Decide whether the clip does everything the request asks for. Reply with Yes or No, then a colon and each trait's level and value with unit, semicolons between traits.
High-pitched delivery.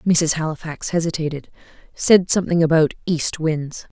No: medium, 160 Hz